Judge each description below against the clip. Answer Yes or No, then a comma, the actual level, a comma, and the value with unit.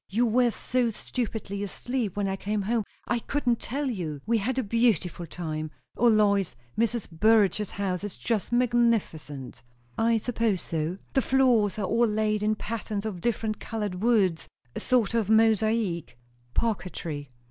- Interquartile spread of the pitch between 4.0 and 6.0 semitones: No, average, 3.4 semitones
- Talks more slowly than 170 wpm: Yes, average, 160 wpm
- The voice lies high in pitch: Yes, high, 215 Hz